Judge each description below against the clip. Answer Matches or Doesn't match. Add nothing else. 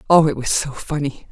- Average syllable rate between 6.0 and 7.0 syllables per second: Doesn't match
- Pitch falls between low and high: Matches